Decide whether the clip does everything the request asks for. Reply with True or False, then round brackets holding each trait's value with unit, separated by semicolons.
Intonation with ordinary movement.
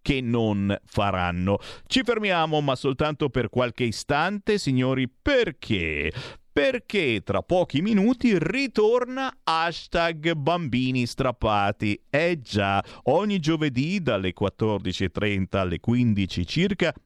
False (9.0 semitones)